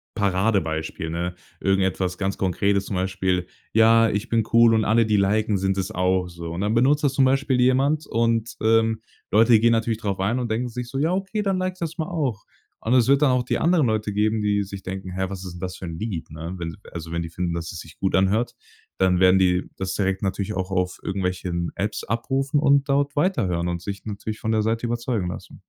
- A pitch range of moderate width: Yes, average, 4.3 semitones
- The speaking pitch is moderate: No, low, 105 Hz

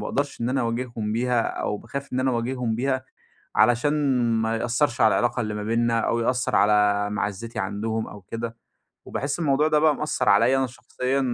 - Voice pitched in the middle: No, low, 120 Hz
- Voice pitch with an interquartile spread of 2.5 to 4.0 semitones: Yes, average, 2.9 semitones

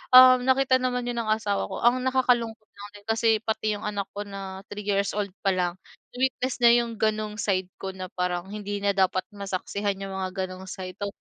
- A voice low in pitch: No, high, 205 Hz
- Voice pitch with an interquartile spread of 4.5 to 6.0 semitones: No, average, 3.2 semitones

